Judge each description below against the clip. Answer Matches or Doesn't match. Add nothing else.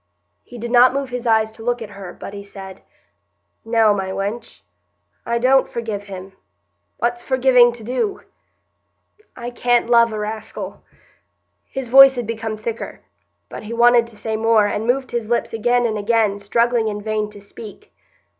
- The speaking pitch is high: Matches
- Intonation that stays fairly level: Matches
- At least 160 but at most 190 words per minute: Matches